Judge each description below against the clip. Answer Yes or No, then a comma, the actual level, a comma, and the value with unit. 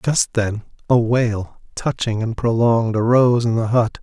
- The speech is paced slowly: No, average, 165 wpm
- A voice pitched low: Yes, low, 115 Hz